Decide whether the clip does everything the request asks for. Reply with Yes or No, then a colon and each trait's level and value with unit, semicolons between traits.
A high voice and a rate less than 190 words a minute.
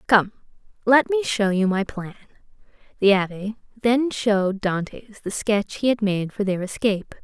Yes: high, 210 Hz; average, 165 wpm